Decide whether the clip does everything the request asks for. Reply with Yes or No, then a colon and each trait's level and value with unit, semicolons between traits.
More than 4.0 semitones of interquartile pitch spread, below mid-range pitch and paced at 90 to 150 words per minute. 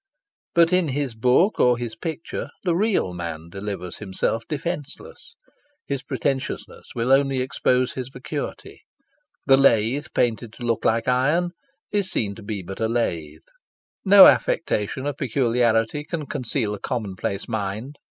Yes: average, 4.9 semitones; low, 125 Hz; average, 140 wpm